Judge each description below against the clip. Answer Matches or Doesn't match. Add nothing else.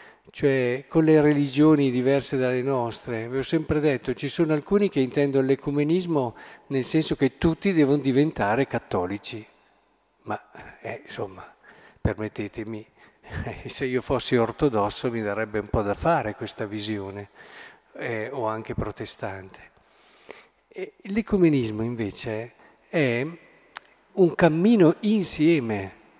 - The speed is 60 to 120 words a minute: Matches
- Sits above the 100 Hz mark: Matches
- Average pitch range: Doesn't match